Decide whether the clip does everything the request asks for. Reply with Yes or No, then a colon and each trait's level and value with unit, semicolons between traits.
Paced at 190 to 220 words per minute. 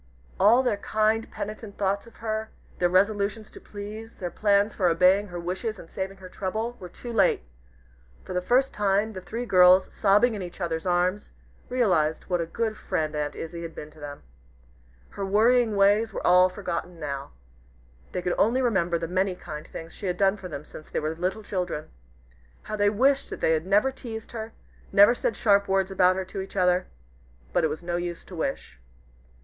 Yes: average, 200 wpm